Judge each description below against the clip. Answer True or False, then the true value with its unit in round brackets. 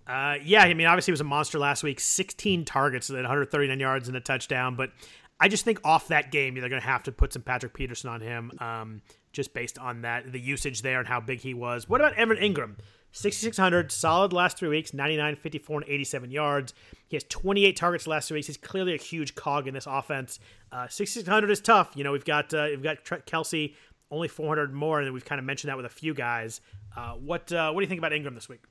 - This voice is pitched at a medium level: True (145 Hz)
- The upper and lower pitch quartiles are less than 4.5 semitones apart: True (4.0 semitones)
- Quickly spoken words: True (240 wpm)